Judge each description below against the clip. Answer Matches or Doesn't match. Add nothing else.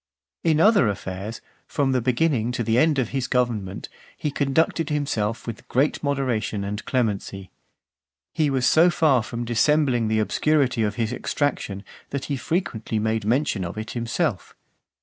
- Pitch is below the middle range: Matches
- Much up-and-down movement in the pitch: Doesn't match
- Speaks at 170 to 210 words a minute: Doesn't match